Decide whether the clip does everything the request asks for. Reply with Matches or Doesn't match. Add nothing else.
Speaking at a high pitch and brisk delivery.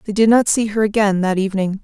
Matches